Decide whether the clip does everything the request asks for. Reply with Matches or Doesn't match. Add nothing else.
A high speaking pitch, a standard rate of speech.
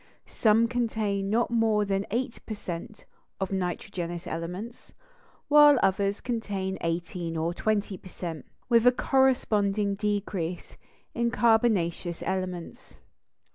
Doesn't match